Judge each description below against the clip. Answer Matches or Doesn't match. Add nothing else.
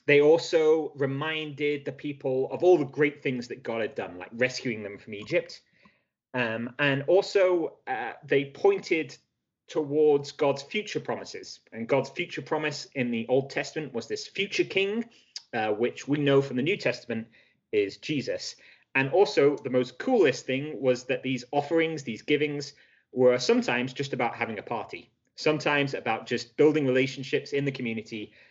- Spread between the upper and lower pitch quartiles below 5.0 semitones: Doesn't match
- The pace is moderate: Matches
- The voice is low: Doesn't match